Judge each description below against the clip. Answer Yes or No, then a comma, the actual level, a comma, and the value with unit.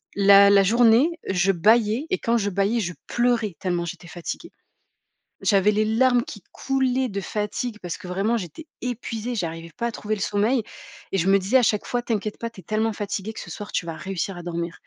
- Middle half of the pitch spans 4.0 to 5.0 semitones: No, average, 3.5 semitones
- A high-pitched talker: Yes, high, 210 Hz